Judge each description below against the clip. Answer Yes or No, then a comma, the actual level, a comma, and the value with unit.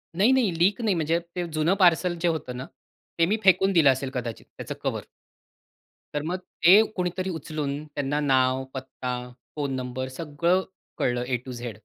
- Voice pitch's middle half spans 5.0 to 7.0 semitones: Yes, wide, 5.4 semitones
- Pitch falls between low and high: Yes, medium, 150 Hz